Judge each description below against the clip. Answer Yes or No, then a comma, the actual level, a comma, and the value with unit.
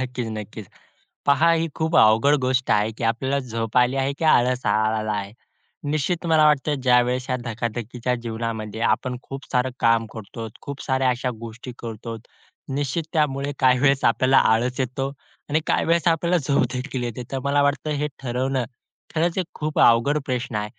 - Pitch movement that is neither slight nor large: Yes, average, 3.5 semitones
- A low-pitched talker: Yes, low, 125 Hz